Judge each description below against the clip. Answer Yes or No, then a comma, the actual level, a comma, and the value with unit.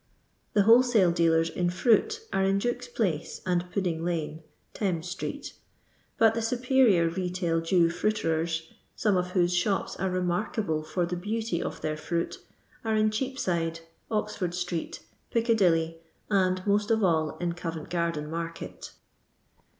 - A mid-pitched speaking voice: Yes, medium, 180 Hz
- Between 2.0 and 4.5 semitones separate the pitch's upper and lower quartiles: Yes, average, 4.2 semitones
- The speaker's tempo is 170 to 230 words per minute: No, average, 145 wpm